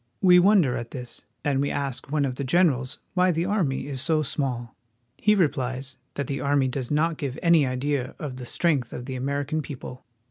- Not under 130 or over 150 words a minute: No, average, 200 wpm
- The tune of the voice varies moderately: Yes, average, 3.5 semitones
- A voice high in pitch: No, medium, 140 Hz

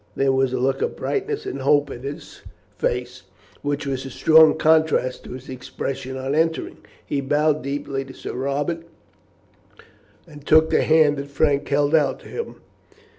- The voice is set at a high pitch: No, medium, 140 Hz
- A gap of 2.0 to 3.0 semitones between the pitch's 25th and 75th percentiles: Yes, average, 2.7 semitones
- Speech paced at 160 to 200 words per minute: Yes, average, 170 wpm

